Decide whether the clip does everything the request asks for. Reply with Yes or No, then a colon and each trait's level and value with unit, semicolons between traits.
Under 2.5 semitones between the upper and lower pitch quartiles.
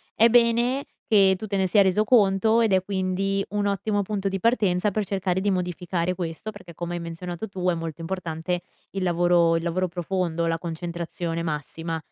No: average, 2.8 semitones